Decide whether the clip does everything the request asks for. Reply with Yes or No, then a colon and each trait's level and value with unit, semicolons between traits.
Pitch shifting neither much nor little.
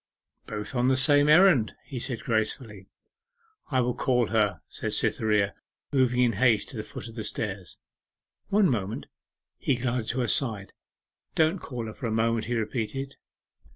Yes: average, 3.2 semitones